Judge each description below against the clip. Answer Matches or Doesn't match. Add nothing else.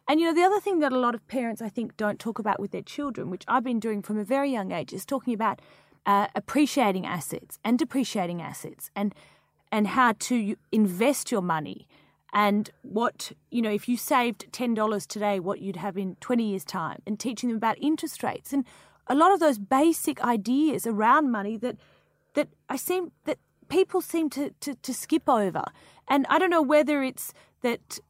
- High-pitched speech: Matches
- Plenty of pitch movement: Doesn't match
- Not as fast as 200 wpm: Doesn't match